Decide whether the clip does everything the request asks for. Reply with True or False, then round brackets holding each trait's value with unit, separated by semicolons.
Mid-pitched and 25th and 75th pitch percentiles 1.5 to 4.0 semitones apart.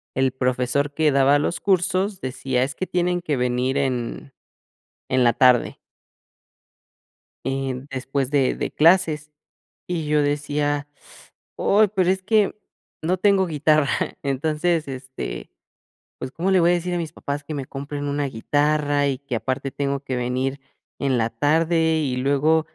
True (145 Hz; 3.5 semitones)